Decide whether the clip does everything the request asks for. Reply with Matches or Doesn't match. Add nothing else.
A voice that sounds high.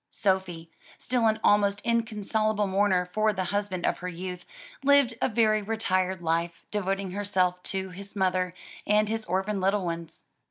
Matches